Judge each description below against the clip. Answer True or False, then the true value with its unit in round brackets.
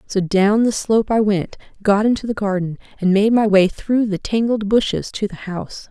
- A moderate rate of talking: False (215 wpm)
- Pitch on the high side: True (205 Hz)